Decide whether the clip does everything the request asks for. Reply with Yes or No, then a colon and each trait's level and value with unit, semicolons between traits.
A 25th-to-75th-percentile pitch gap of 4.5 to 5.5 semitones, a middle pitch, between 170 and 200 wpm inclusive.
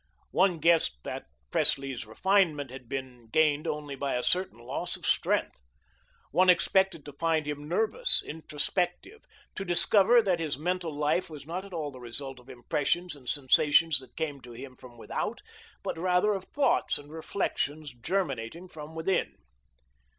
No: average, 4.8 semitones; medium, 155 Hz; average, 160 wpm